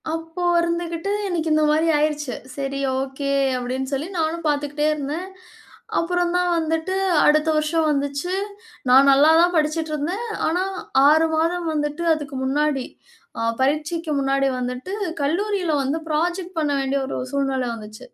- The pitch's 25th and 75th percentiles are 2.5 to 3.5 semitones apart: Yes, average, 3.2 semitones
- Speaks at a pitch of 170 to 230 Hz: No, very high, 305 Hz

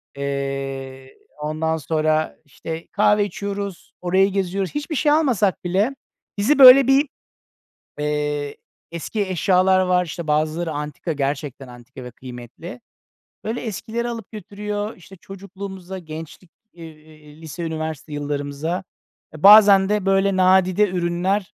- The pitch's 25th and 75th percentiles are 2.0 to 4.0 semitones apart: No, average, 4.9 semitones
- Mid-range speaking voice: Yes, medium, 175 Hz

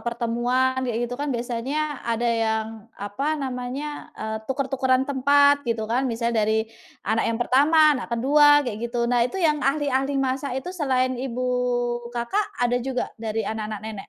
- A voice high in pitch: Yes, very high, 255 Hz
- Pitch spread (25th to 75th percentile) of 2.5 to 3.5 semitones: Yes, average, 3.1 semitones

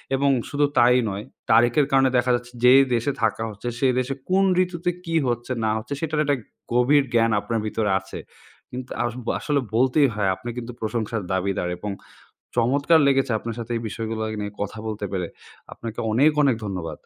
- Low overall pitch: Yes, low, 120 Hz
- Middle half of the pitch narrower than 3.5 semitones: No, average, 3.9 semitones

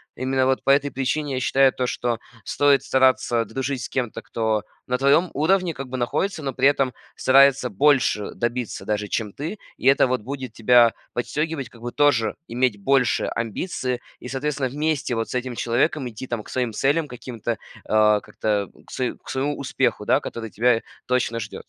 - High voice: No, low, 130 Hz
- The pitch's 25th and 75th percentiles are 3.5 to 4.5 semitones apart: No, average, 2.8 semitones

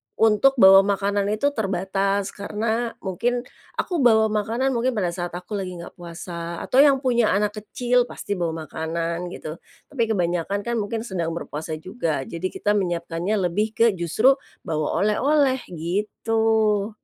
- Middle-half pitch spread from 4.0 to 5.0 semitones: Yes, average, 4.5 semitones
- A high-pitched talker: Yes, high, 200 Hz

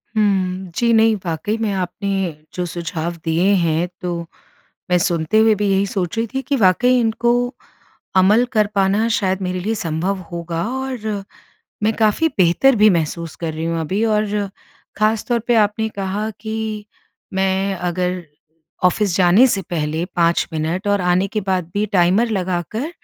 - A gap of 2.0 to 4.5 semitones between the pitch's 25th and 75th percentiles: Yes, average, 3.6 semitones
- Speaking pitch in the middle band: No, high, 195 Hz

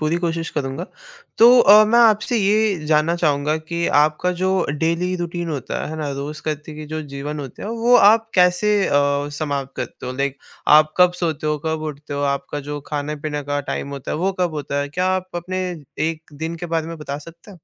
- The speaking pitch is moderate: Yes, medium, 160 Hz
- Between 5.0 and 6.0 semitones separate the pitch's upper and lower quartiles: No, average, 3.5 semitones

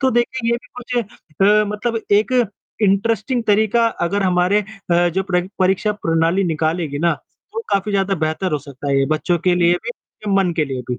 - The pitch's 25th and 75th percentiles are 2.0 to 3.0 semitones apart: No, average, 4.4 semitones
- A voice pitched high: Yes, high, 195 Hz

